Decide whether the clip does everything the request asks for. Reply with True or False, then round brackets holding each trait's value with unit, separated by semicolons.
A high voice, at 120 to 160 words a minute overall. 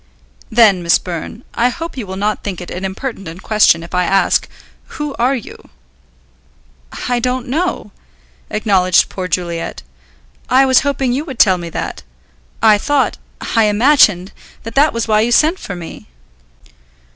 True (215 Hz; 155 wpm)